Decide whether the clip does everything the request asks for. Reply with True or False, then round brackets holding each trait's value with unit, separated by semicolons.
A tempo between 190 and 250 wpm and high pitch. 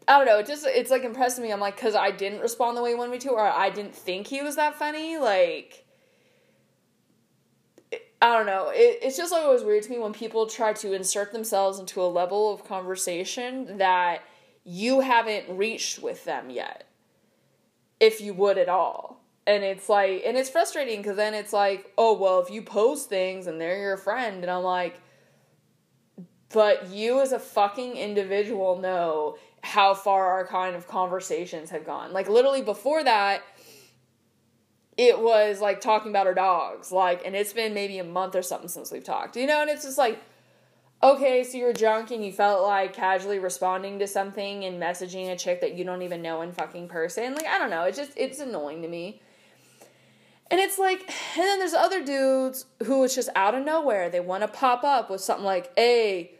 True (200 wpm; 205 Hz)